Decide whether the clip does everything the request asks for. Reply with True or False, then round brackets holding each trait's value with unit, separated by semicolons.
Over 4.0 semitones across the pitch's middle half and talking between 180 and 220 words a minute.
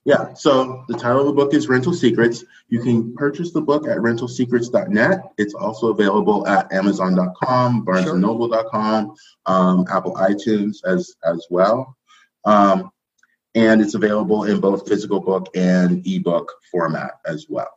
False (5.3 semitones; 145 wpm)